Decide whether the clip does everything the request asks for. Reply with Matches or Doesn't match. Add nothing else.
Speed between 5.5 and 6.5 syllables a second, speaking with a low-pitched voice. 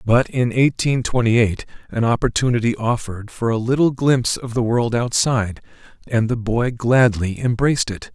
Doesn't match